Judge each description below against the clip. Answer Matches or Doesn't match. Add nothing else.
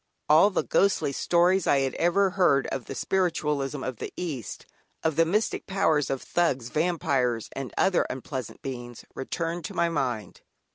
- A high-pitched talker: Doesn't match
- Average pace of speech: Matches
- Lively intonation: Doesn't match